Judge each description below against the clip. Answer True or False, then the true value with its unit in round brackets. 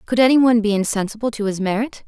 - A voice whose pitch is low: False (220 Hz)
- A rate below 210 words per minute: True (200 wpm)